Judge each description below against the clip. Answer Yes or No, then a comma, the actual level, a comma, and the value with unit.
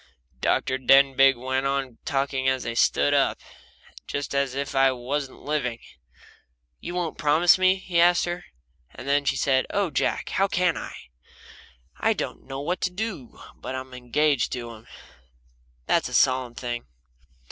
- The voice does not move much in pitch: No, average, 3.6 semitones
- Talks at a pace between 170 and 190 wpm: No, average, 155 wpm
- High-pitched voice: No, low, 135 Hz